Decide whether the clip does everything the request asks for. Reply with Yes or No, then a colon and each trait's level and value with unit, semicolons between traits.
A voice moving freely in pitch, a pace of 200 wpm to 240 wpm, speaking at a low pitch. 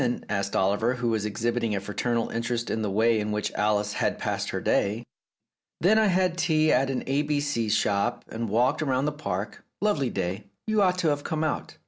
Yes: wide, 6.0 semitones; fast, 205 wpm; low, 120 Hz